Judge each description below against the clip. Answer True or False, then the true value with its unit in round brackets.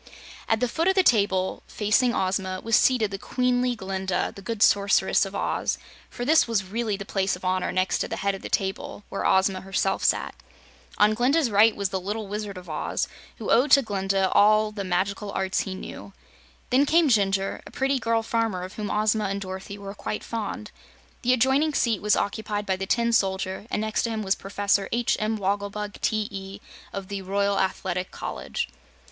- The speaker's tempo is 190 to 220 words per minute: True (200 wpm)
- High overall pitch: True (205 Hz)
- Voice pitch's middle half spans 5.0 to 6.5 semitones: False (2.8 semitones)